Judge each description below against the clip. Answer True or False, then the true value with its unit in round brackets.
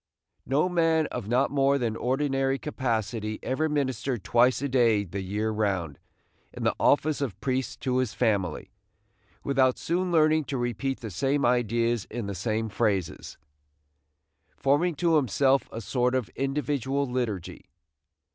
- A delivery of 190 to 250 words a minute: False (145 wpm)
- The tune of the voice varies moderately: True (4.0 semitones)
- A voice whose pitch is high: False (130 Hz)